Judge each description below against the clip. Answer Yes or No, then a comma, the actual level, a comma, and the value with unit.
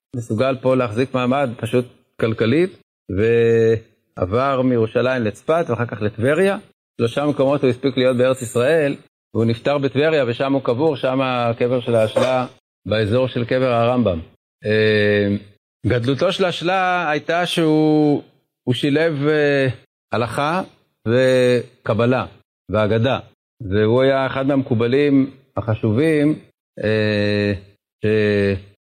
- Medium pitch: No, low, 125 Hz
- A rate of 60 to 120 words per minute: Yes, slow, 100 wpm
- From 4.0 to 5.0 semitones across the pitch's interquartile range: No, average, 3.6 semitones